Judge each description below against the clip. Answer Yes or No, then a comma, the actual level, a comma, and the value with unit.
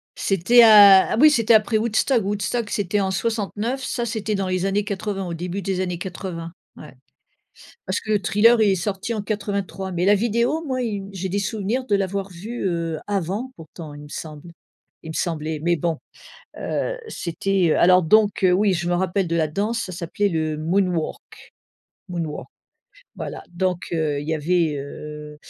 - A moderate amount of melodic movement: Yes, average, 3.7 semitones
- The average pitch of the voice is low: No, high, 190 Hz